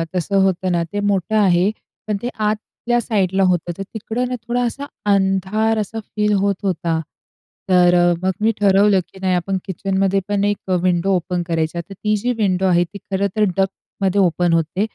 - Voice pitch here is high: Yes, high, 195 Hz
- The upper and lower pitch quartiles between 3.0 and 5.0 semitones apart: No, narrow, 2.5 semitones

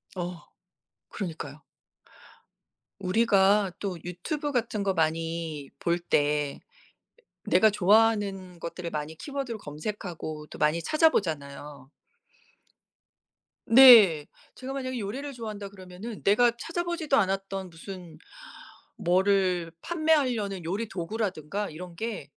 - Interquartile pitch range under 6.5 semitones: Yes, average, 5.2 semitones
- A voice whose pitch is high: Yes, high, 195 Hz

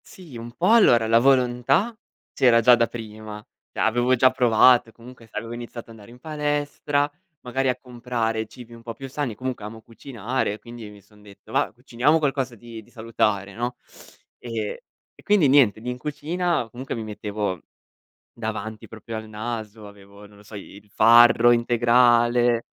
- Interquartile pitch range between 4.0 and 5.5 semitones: No, narrow, 2.6 semitones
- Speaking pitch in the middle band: No, low, 120 Hz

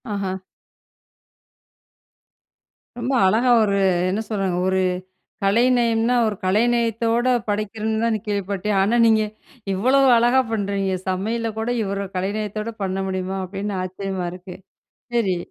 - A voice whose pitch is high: Yes, high, 210 Hz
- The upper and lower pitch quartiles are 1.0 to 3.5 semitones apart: Yes, average, 2.9 semitones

